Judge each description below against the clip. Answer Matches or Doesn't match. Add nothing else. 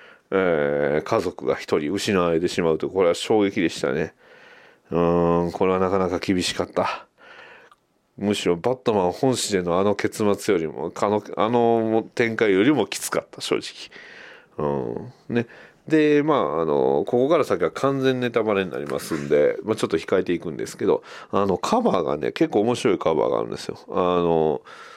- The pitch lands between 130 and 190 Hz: Doesn't match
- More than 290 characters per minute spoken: Matches